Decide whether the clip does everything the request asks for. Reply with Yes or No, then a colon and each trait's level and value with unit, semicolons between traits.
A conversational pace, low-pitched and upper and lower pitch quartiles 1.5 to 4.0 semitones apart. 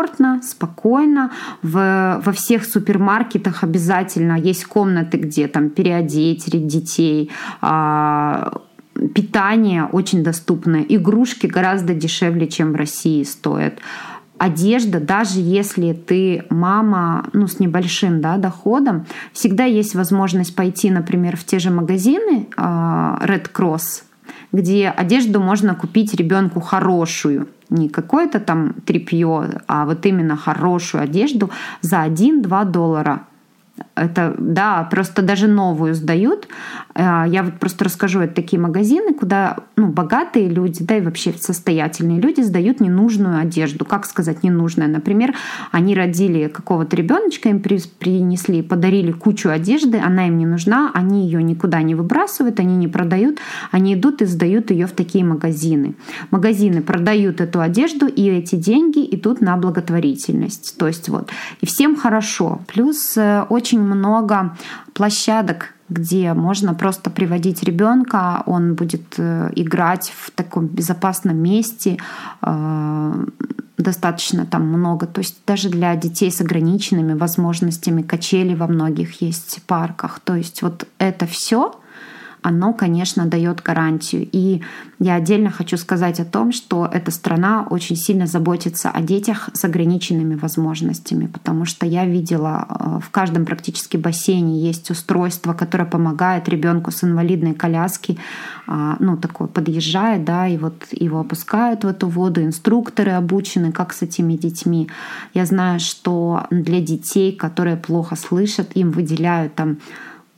No: average, 130 wpm; medium, 180 Hz; average, 3.2 semitones